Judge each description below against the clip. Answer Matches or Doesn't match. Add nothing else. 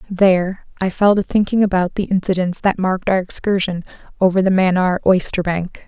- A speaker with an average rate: Matches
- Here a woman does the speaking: Matches